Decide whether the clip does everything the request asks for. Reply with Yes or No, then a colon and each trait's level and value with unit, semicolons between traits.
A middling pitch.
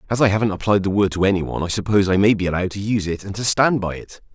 No: low, 100 Hz